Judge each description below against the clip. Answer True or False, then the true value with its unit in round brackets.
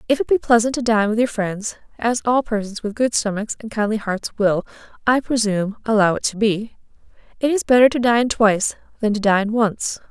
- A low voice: False (220 Hz)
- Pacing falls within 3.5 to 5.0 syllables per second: False (5.4 syllables/s)